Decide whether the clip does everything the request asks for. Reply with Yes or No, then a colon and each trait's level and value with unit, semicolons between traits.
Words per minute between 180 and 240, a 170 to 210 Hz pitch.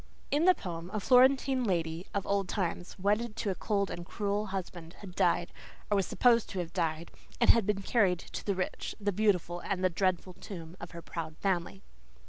Yes: average, 195 wpm; high, 190 Hz